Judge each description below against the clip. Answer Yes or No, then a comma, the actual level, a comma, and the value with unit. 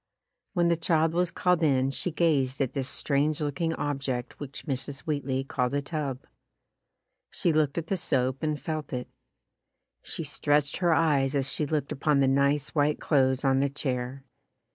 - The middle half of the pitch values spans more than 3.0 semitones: No, average, 2.7 semitones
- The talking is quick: No, average, 175 wpm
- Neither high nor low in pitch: Yes, medium, 145 Hz